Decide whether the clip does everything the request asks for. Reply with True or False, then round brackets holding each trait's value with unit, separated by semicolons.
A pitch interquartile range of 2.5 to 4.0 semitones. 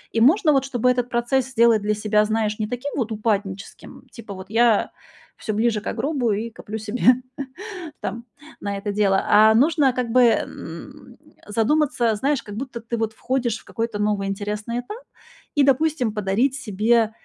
True (3.1 semitones)